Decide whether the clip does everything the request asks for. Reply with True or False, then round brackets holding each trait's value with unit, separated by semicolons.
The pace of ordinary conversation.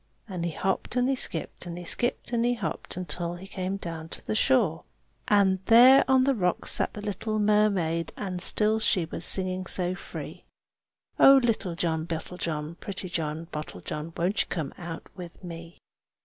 True (175 wpm)